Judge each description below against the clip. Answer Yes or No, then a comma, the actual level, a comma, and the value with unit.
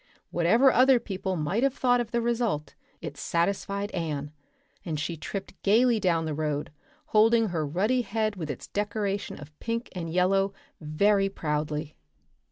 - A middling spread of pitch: No, wide, 6.0 semitones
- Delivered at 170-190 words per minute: No, average, 155 wpm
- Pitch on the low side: No, high, 195 Hz